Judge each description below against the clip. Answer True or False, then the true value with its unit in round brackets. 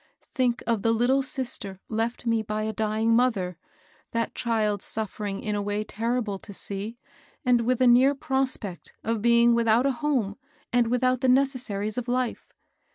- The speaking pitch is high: True (230 Hz)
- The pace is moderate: True (170 wpm)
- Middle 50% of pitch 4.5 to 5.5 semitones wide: False (2.8 semitones)